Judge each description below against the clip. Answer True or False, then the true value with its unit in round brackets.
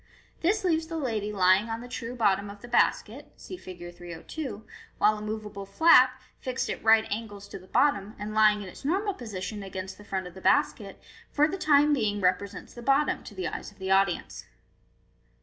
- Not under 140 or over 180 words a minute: False (200 wpm)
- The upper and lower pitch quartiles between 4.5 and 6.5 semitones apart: True (5.0 semitones)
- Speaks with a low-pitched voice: False (215 Hz)